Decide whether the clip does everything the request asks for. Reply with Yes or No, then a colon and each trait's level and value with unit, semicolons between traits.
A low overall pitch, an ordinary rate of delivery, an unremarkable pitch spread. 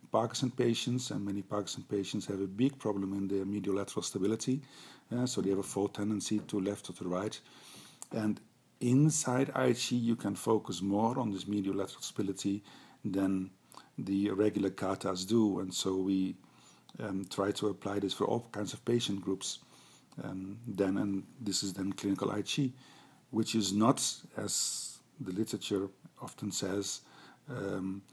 Yes: low, 100 Hz; average, 155 wpm; average, 3.2 semitones